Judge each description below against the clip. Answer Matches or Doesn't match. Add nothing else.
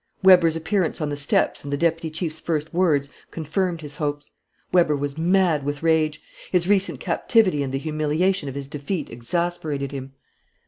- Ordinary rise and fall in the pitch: Matches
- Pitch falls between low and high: Matches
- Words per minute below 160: Doesn't match